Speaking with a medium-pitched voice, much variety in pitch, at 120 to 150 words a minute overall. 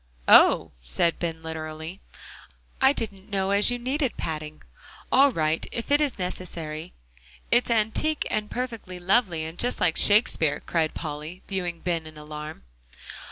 Yes: medium, 180 Hz; wide, 6.2 semitones; average, 145 wpm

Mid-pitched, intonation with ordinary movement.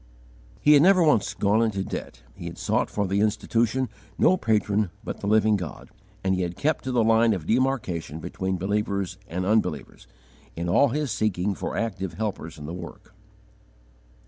No: low, 105 Hz; average, 3.9 semitones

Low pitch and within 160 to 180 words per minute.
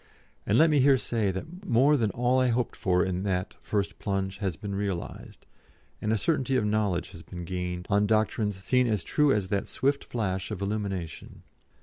No: low, 105 Hz; average, 195 wpm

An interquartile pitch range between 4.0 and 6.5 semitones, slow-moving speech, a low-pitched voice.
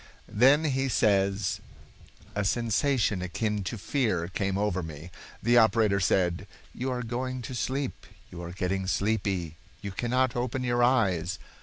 No: average, 4.7 semitones; average, 145 wpm; low, 105 Hz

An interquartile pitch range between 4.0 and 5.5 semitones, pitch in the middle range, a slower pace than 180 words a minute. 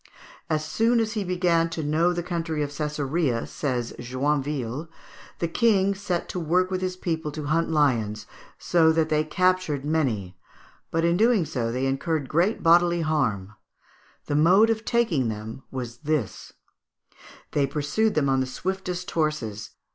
Yes: average, 4.7 semitones; medium, 155 Hz; average, 155 wpm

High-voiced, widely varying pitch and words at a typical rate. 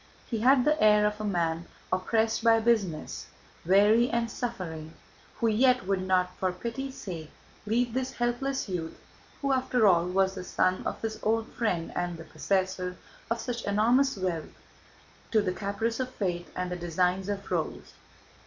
No: high, 205 Hz; average, 4.4 semitones; average, 165 wpm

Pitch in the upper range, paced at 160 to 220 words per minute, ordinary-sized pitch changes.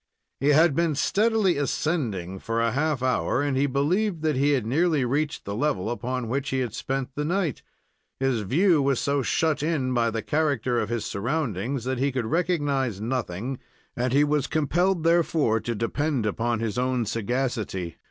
No: low, 135 Hz; average, 180 wpm; average, 4.4 semitones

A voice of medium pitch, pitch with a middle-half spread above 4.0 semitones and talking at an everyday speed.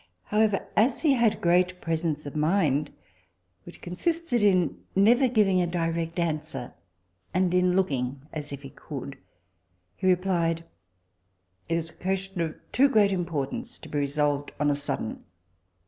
Yes: medium, 170 Hz; average, 4.4 semitones; average, 145 wpm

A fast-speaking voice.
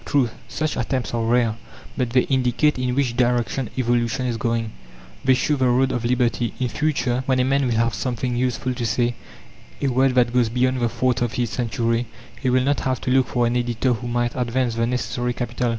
Yes: fast, 215 wpm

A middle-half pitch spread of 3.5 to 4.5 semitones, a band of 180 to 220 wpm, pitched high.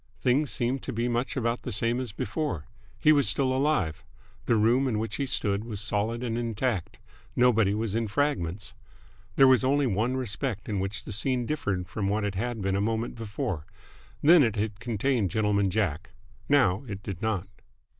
No: average, 4.0 semitones; average, 185 wpm; low, 110 Hz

